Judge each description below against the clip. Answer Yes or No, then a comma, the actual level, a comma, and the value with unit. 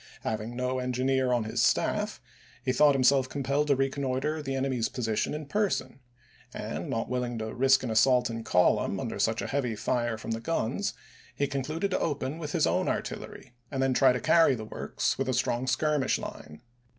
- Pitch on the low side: Yes, low, 130 Hz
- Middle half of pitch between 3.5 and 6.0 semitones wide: No, average, 2.7 semitones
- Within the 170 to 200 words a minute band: Yes, average, 190 wpm